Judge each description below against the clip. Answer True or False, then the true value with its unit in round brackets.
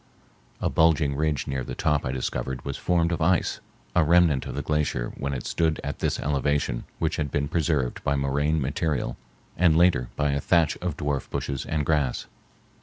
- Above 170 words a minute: True (185 wpm)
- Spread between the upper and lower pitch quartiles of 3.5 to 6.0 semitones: False (2.8 semitones)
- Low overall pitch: True (75 Hz)